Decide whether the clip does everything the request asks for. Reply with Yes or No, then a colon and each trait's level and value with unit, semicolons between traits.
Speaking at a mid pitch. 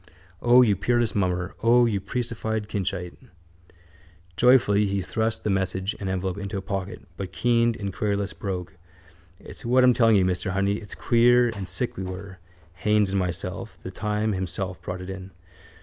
No: low, 100 Hz